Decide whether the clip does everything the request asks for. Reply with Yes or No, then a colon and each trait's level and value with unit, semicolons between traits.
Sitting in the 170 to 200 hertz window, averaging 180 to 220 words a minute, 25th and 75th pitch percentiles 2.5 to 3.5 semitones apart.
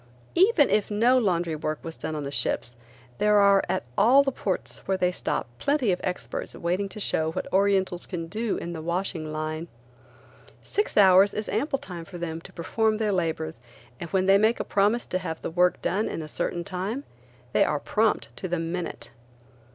No: medium, 185 Hz; average, 200 wpm; average, 4.1 semitones